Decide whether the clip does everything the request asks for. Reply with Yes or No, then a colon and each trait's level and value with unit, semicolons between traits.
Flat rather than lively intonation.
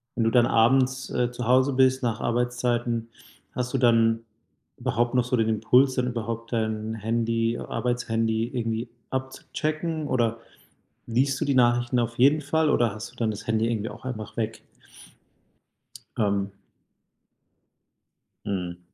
Yes: narrow, 2.1 semitones